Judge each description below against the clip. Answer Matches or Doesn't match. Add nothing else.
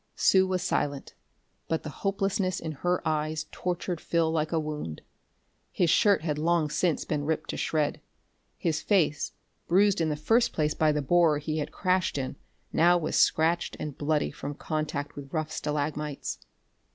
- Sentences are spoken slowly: Doesn't match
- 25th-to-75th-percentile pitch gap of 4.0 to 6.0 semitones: Doesn't match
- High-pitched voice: Doesn't match